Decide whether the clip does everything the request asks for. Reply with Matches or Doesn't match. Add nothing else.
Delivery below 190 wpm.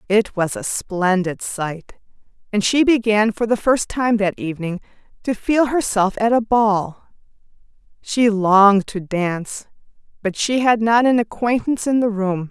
Matches